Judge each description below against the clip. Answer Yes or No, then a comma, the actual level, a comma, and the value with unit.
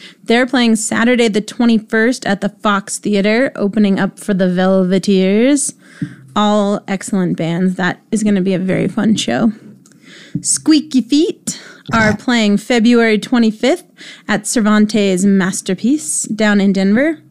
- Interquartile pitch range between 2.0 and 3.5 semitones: Yes, average, 3.2 semitones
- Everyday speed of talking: No, slow, 130 wpm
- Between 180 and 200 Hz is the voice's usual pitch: No, high, 210 Hz